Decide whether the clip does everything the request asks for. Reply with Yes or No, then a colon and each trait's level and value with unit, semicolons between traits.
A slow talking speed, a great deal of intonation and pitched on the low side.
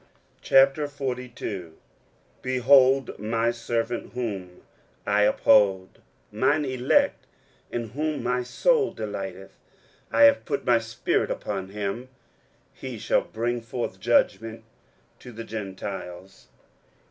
No: slow, 100 wpm; average, 3.8 semitones; low, 120 Hz